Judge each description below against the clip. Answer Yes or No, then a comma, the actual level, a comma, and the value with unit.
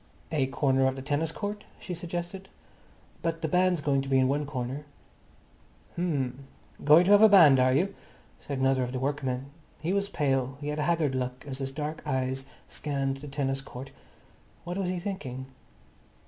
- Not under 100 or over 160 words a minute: No, average, 185 wpm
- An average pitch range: Yes, average, 4.2 semitones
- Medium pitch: Yes, medium, 145 Hz